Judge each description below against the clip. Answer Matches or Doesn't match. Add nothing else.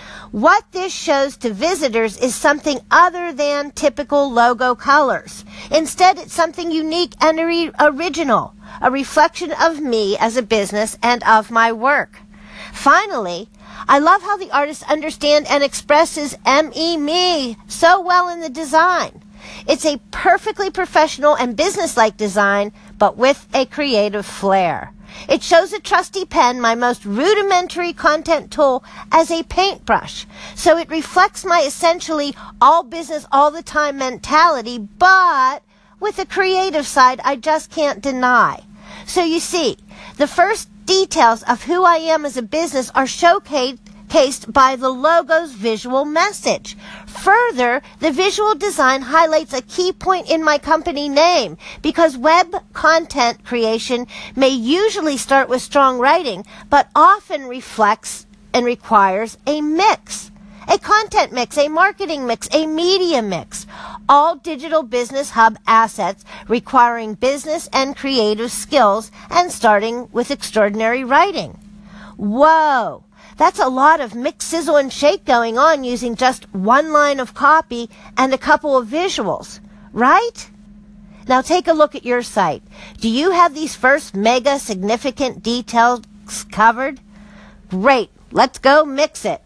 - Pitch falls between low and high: Doesn't match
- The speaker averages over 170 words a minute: Doesn't match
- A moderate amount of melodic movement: Doesn't match